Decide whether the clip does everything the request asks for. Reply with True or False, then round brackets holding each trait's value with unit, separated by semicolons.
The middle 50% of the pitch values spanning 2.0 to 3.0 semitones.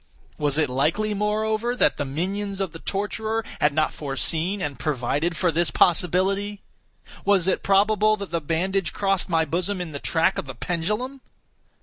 False (4.3 semitones)